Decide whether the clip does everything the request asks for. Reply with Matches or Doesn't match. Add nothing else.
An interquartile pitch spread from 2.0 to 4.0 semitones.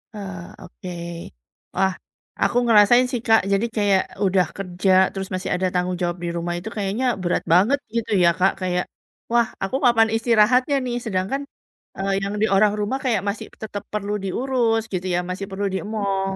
Matches